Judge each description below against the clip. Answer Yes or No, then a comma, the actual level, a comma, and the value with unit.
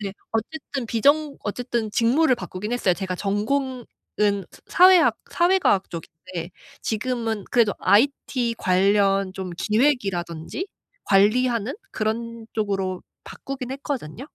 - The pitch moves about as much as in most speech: Yes, average, 4.7 semitones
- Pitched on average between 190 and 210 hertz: No, high, 220 Hz